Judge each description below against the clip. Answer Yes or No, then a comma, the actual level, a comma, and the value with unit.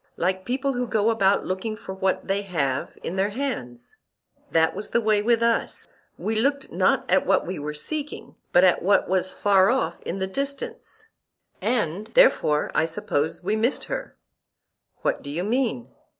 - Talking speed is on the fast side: No, average, 165 wpm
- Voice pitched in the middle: No, high, 200 Hz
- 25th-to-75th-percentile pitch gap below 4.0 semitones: No, average, 4.8 semitones